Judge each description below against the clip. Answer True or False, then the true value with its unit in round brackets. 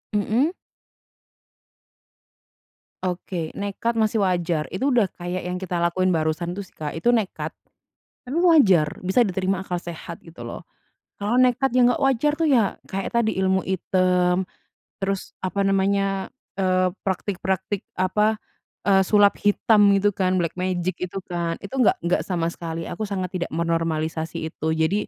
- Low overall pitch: False (190 Hz)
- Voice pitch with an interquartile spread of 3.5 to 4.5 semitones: False (2.9 semitones)